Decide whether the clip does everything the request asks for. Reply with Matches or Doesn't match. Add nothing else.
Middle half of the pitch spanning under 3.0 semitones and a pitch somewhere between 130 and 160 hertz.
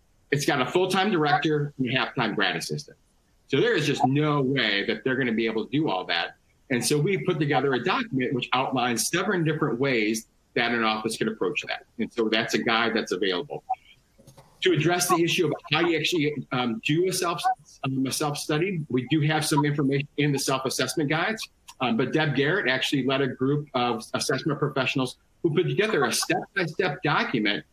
Doesn't match